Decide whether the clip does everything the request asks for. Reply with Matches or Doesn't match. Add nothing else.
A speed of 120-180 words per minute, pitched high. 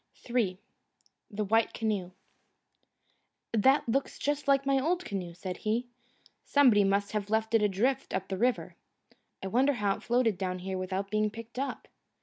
Matches